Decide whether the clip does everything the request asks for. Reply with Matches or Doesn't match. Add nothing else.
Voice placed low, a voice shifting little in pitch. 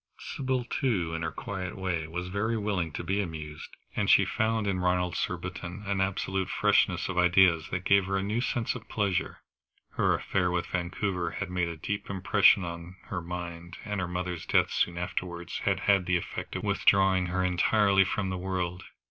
Matches